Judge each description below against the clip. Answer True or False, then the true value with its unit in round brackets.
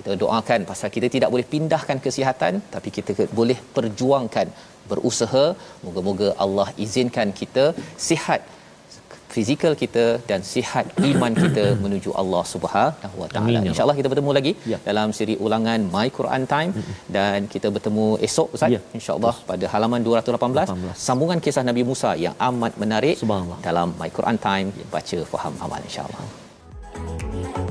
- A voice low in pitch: True (115 Hz)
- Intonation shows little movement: False (4.4 semitones)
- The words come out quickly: True (135 wpm)